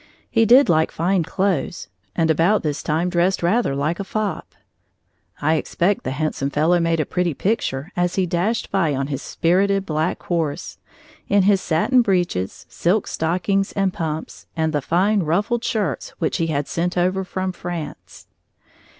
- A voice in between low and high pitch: Yes, medium, 175 Hz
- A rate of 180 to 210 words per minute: No, average, 165 wpm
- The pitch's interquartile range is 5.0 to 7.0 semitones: No, average, 3.6 semitones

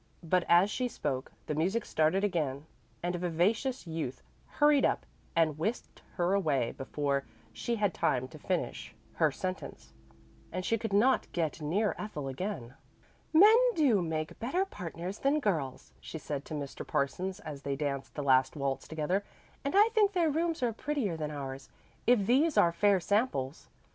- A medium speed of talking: Yes, average, 170 wpm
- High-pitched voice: No, medium, 175 Hz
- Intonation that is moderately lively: No, wide, 7.5 semitones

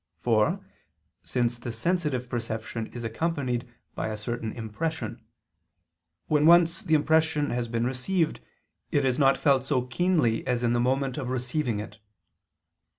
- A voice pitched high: No, low, 125 Hz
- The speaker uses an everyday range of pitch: Yes, average, 4.3 semitones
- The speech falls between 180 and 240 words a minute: No, average, 145 wpm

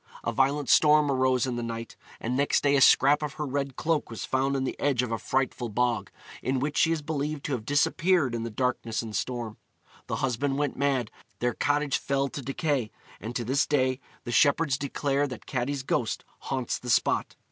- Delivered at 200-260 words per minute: Yes, fast, 205 wpm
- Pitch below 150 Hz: Yes, low, 135 Hz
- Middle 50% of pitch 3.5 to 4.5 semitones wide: No, average, 2.8 semitones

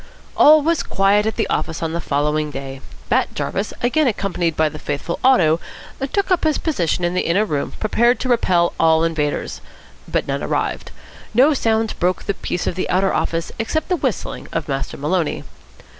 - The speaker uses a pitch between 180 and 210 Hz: Yes, medium, 185 Hz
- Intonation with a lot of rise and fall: Yes, wide, 6.8 semitones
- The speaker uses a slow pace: No, average, 185 wpm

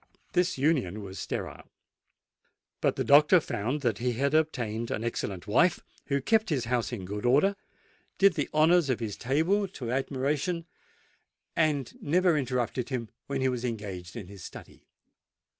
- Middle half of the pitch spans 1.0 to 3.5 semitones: No, average, 5.2 semitones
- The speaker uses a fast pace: No, average, 150 wpm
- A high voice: No, low, 130 Hz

